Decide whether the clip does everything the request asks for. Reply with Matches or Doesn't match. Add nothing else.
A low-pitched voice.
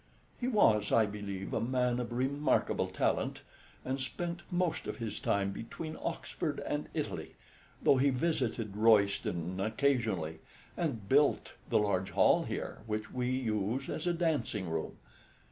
Matches